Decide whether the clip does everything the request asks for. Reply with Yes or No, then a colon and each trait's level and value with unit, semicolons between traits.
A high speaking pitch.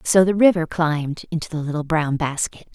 No: medium, 160 Hz